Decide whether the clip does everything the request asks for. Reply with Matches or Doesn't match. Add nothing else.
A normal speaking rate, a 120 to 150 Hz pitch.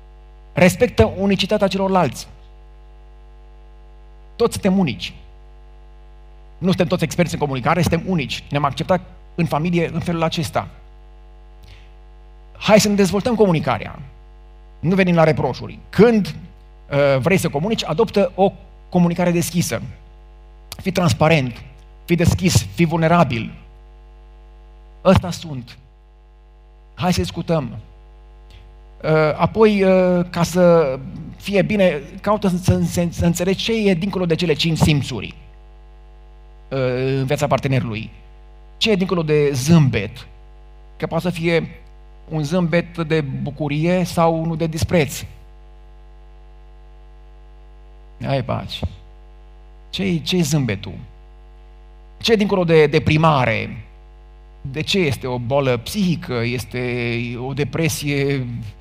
Doesn't match